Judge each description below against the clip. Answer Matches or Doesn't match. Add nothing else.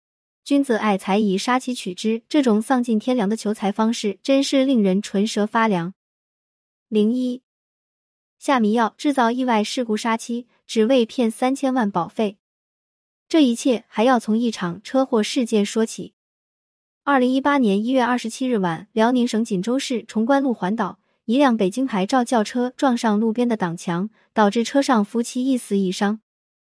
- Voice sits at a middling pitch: Doesn't match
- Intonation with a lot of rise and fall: Doesn't match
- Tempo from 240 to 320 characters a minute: Matches